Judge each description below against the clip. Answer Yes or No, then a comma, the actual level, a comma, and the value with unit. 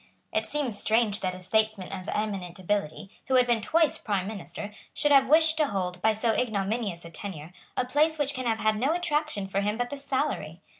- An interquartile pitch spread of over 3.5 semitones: Yes, wide, 5.5 semitones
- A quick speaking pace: Yes, fast, 210 wpm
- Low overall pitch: No, high, 220 Hz